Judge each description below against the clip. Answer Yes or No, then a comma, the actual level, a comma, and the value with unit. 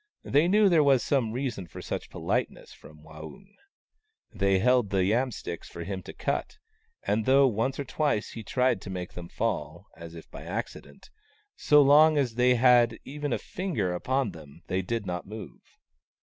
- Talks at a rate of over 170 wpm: Yes, average, 190 wpm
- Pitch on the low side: Yes, low, 115 Hz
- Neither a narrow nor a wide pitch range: No, wide, 6.8 semitones